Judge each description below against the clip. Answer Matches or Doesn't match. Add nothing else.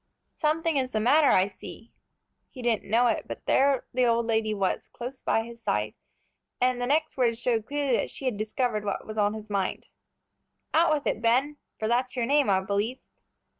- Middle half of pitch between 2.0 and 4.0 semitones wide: Matches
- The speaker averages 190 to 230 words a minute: Matches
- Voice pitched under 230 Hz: Doesn't match